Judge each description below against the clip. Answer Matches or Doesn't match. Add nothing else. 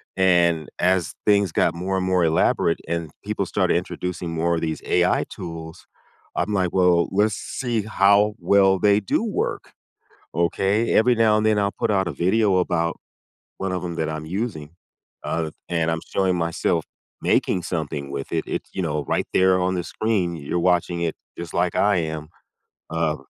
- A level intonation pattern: Doesn't match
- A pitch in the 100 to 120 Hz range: Doesn't match